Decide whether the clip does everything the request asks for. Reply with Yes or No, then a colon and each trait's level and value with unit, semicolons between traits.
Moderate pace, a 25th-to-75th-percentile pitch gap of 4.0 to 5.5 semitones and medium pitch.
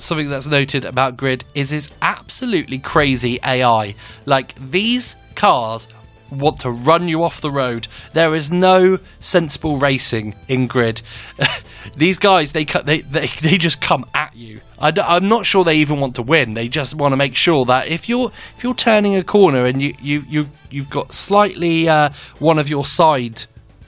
Yes: average, 180 wpm; average, 4.7 semitones; medium, 145 Hz